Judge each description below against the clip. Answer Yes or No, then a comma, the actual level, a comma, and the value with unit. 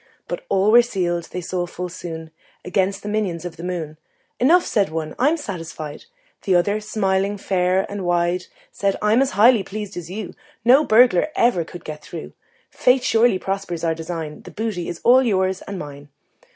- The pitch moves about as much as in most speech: Yes, average, 3.8 semitones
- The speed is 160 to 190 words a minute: Yes, average, 180 wpm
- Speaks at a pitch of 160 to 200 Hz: Yes, high, 190 Hz